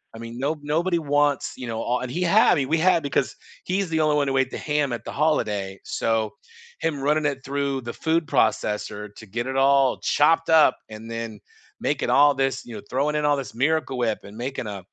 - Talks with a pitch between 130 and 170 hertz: Yes, low, 135 Hz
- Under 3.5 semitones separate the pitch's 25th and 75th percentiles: No, average, 4.3 semitones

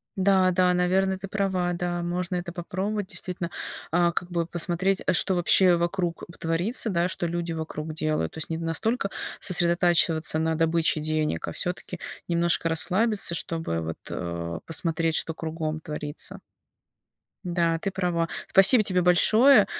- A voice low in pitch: No, medium, 175 Hz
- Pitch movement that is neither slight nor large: No, narrow, 2.2 semitones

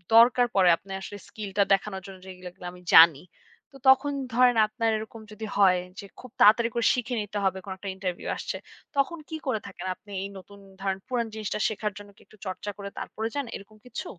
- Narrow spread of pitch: No, average, 3.3 semitones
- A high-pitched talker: Yes, high, 210 Hz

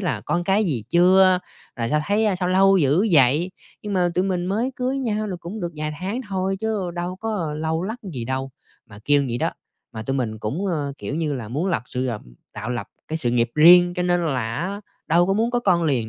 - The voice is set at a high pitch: No, medium, 175 Hz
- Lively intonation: Yes, wide, 6.0 semitones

